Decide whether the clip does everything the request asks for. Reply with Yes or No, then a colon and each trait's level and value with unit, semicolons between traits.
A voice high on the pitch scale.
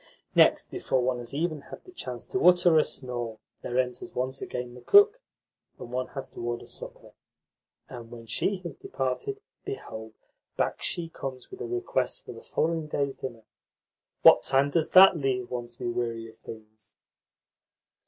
No: low, 130 Hz